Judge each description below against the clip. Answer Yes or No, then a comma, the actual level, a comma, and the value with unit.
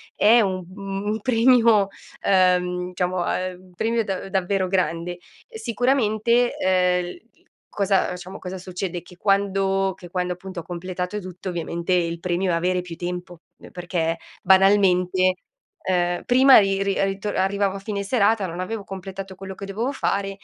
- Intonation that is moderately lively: No, narrow, 1.8 semitones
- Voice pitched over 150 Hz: Yes, high, 190 Hz